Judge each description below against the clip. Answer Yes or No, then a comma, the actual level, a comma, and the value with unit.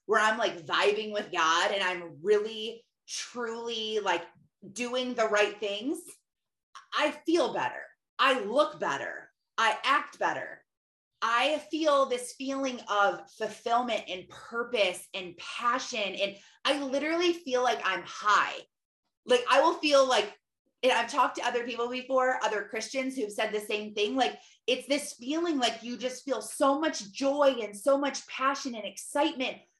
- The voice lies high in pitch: Yes, high, 245 Hz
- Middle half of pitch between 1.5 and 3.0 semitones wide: No, average, 4.6 semitones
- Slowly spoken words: No, average, 155 wpm